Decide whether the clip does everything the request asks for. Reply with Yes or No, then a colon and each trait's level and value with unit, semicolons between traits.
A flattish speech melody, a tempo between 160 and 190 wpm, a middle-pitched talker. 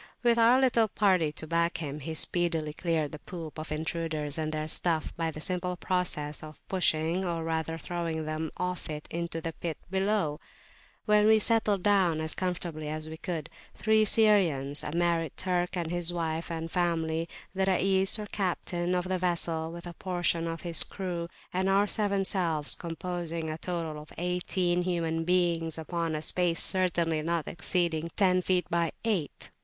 Yes: narrow, 2.3 semitones; average, 175 wpm; medium, 170 Hz